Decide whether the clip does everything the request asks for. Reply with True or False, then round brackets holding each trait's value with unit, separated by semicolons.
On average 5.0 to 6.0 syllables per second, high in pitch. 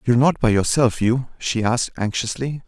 False (5.4 syllables/s; 120 Hz)